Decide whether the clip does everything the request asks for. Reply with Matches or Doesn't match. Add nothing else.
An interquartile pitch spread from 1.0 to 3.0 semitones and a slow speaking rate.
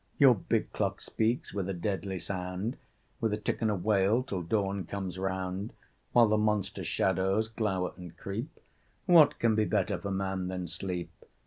Doesn't match